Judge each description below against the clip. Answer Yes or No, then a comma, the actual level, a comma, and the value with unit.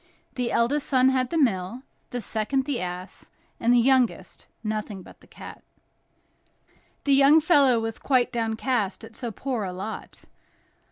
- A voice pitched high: Yes, high, 240 Hz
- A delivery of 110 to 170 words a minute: Yes, average, 155 wpm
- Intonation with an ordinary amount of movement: Yes, average, 3.5 semitones